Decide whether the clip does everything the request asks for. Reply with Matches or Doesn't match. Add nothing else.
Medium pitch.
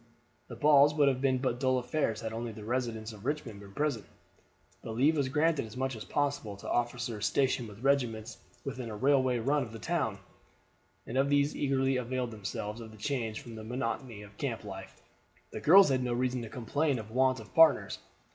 Doesn't match